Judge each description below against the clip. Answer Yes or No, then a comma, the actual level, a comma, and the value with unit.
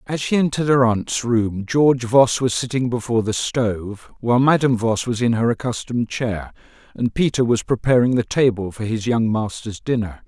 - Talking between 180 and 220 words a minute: Yes, average, 185 wpm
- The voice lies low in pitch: Yes, low, 120 Hz